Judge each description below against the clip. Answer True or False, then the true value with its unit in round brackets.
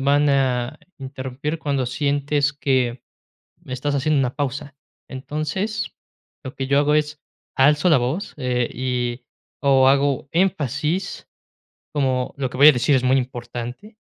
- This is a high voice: False (140 Hz)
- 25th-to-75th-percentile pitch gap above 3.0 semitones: False (2.5 semitones)